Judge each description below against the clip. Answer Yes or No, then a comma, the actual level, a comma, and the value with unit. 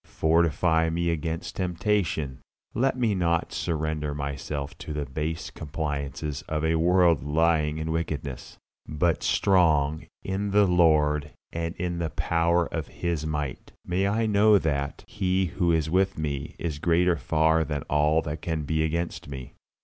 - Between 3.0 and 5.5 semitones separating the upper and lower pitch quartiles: No, narrow, 2.6 semitones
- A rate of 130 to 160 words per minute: Yes, average, 150 wpm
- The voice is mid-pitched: No, very low, 80 Hz